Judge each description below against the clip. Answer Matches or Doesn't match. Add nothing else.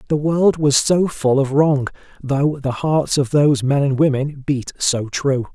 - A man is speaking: Matches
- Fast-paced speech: Doesn't match